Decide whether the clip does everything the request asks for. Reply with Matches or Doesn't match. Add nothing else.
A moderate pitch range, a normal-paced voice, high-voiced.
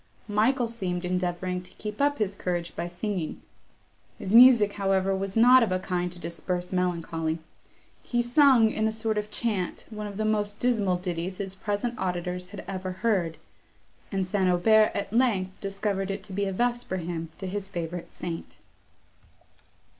Matches